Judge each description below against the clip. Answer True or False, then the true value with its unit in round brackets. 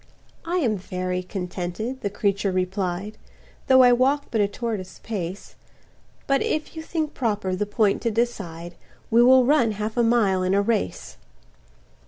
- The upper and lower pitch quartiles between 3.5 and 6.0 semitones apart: True (4.5 semitones)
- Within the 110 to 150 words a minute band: False (160 wpm)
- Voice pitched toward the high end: True (210 Hz)